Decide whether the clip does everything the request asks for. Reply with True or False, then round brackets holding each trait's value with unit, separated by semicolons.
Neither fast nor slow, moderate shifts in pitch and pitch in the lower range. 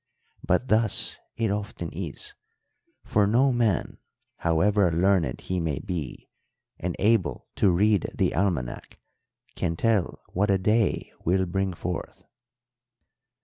False (120 wpm; 3.6 semitones; 95 Hz)